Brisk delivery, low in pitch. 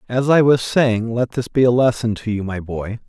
Yes: fast, 255 wpm; low, 115 Hz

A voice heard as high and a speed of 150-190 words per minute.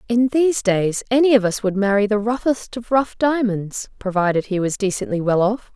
No: high, 215 Hz; average, 200 wpm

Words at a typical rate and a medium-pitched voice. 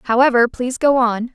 No: average, 180 wpm; high, 245 Hz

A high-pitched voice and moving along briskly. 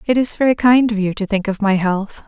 Yes: high, 215 Hz; fast, 290 wpm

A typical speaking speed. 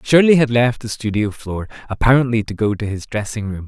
No: fast, 210 wpm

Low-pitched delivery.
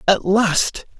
No: high, 195 Hz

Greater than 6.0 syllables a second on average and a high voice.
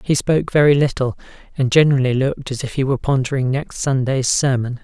No: 6.2 syllables/s; low, 135 Hz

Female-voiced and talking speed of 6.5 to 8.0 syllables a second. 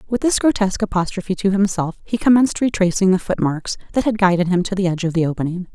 Yes: female; 6.8 syllables/s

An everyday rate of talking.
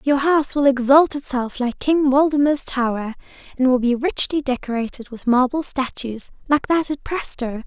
Yes: average, 165 wpm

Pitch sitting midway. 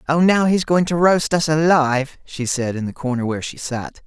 Yes: medium, 150 Hz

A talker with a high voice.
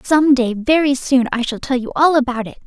Yes: very high, 260 Hz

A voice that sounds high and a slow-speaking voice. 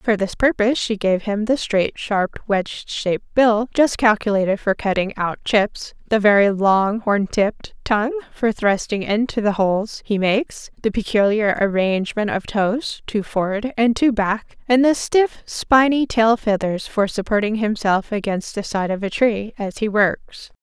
No: high, 215 Hz; average, 170 wpm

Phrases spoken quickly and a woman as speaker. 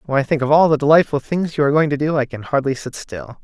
No: fast, 315 wpm; male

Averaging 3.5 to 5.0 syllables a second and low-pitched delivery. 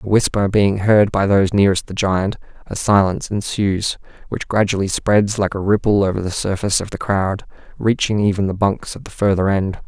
No: 5.4 syllables/s; low, 100 Hz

